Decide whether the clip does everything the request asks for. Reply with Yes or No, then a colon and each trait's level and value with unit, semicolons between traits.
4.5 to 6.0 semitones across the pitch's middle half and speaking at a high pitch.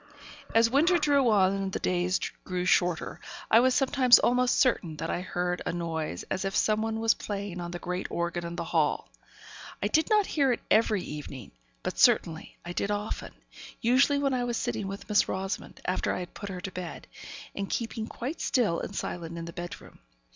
Yes: wide, 5.4 semitones; high, 195 Hz